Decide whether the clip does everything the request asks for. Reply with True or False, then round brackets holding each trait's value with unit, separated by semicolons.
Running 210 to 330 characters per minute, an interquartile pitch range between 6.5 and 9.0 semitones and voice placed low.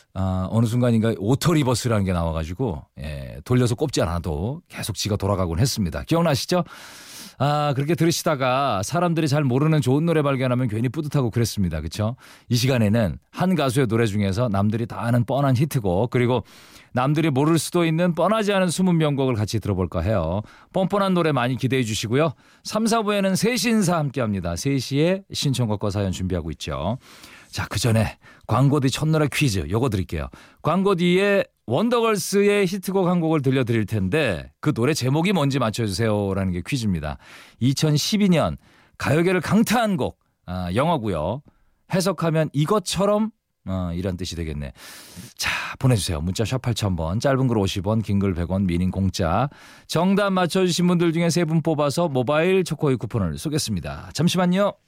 False (355 characters per minute; 8.2 semitones; 130 Hz)